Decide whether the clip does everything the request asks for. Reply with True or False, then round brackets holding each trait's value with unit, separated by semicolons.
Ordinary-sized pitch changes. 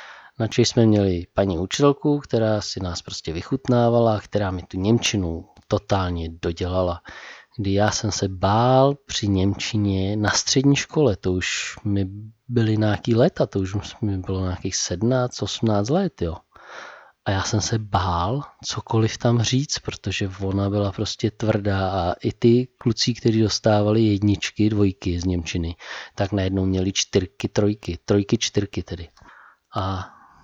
True (3.2 semitones)